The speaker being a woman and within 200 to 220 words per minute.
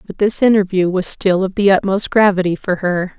Yes: female; fast, 205 wpm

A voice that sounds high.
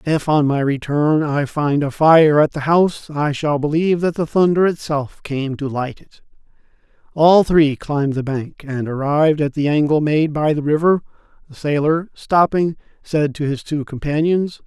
No: medium, 150 Hz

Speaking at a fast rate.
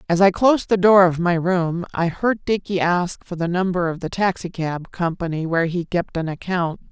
Yes: fast, 210 wpm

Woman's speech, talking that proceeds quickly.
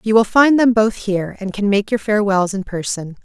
Yes: female; fast, 240 wpm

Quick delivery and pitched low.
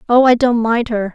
No: fast, 260 wpm; high, 235 Hz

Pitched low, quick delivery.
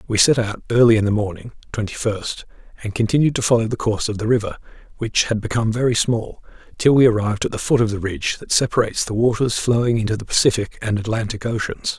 Yes: low, 110 Hz; fast, 215 wpm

